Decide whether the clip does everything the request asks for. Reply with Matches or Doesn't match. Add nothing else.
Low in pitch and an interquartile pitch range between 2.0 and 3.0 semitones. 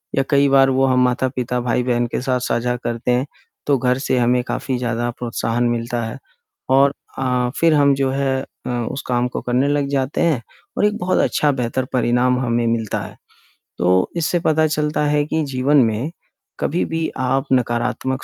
Matches